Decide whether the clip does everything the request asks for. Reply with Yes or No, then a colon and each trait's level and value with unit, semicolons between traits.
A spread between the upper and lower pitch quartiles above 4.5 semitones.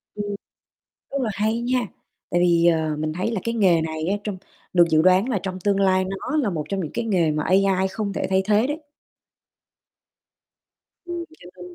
No: average, 3.7 semitones